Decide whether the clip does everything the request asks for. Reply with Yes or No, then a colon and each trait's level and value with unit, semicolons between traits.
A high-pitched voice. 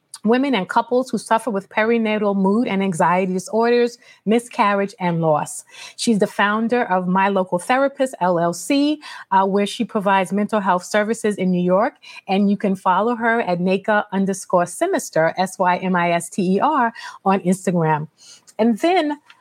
Yes: high, 205 Hz